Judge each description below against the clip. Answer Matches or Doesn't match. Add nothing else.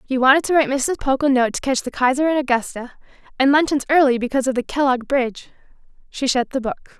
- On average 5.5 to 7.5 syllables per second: Matches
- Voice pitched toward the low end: Doesn't match